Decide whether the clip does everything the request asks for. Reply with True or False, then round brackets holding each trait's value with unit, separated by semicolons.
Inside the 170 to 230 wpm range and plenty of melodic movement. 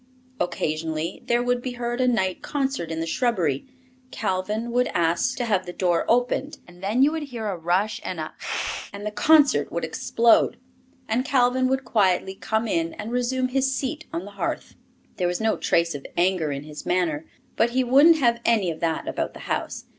True (200 wpm; 6.1 semitones)